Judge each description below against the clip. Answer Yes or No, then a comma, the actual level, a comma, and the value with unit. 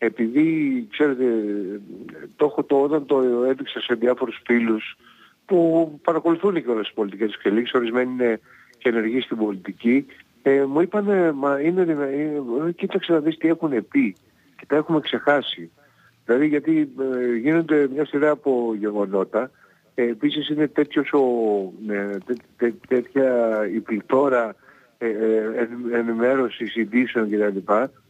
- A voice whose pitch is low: Yes, low, 130 Hz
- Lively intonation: No, average, 4.8 semitones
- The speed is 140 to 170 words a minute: Yes, average, 145 wpm